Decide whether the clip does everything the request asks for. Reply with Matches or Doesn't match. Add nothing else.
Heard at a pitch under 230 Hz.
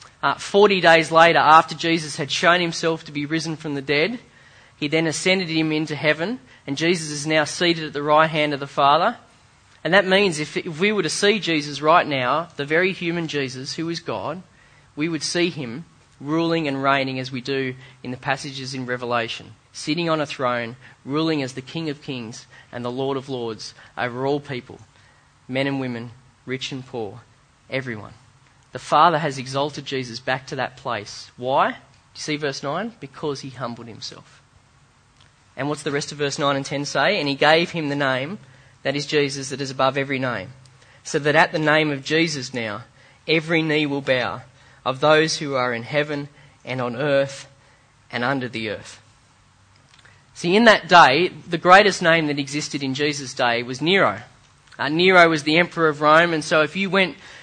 Matches